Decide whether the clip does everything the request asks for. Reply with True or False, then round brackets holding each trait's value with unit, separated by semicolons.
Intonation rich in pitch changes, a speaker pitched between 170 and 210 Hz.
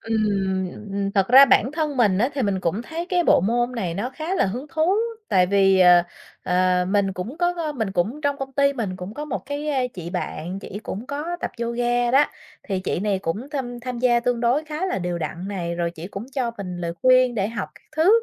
False (6.5 semitones; 235 Hz)